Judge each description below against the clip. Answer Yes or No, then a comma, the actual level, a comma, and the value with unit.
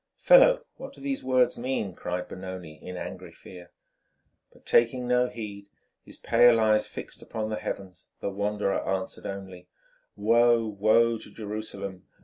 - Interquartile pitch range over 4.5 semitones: No, average, 3.8 semitones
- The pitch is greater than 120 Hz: No, low, 105 Hz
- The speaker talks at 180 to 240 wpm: No, average, 145 wpm